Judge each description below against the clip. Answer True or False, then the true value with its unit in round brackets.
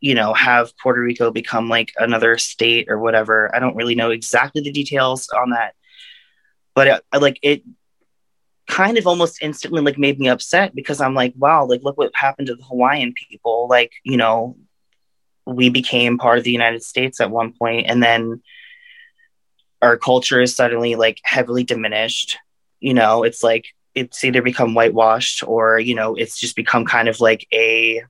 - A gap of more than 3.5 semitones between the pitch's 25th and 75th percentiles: False (3.0 semitones)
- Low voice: True (120 Hz)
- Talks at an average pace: True (180 wpm)